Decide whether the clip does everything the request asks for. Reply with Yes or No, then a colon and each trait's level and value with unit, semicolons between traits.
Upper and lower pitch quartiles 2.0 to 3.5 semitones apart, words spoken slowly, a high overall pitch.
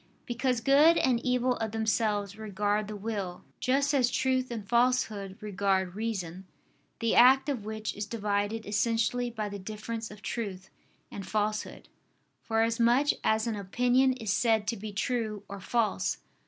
No: average, 2.9 semitones; average, 155 wpm; high, 220 Hz